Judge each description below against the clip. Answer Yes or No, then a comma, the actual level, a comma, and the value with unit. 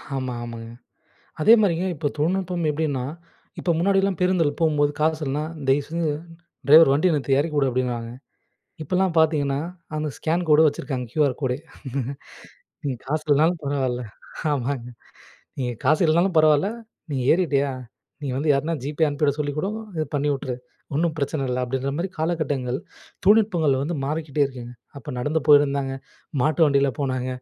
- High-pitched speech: No, medium, 145 Hz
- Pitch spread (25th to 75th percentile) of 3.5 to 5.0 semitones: No, average, 3.0 semitones